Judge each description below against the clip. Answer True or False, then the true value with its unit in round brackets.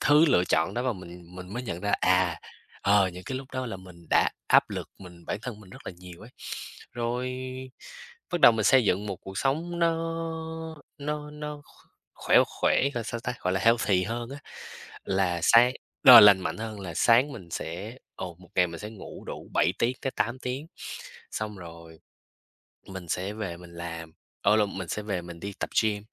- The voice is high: False (105 Hz)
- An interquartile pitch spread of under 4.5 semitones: False (5.3 semitones)